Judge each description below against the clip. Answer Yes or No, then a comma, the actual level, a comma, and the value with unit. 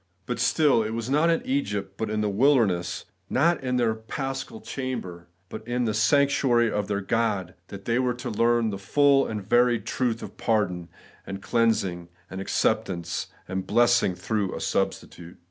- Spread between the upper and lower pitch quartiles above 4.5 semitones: No, average, 4.2 semitones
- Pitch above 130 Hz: No, low, 115 Hz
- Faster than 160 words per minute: Yes, average, 175 wpm